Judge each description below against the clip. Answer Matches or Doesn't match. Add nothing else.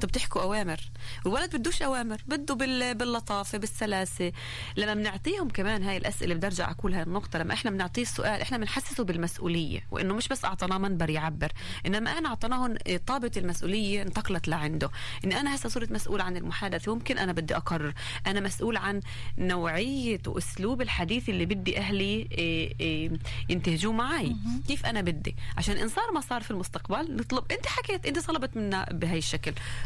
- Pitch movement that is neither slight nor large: Doesn't match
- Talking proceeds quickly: Matches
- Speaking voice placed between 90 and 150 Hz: Doesn't match